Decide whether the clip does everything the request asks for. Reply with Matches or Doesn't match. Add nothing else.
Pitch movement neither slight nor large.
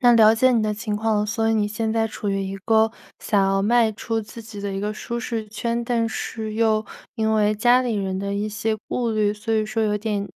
Doesn't match